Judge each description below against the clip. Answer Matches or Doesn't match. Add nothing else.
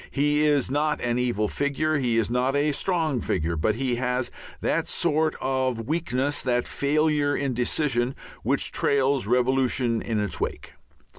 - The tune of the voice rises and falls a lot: Doesn't match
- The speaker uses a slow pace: Doesn't match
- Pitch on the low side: Matches